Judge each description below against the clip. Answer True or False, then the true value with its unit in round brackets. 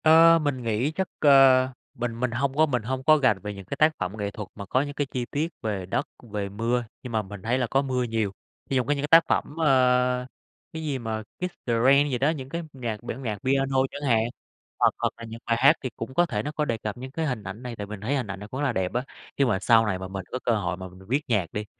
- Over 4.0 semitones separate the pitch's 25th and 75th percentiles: True (4.4 semitones)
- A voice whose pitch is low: True (125 Hz)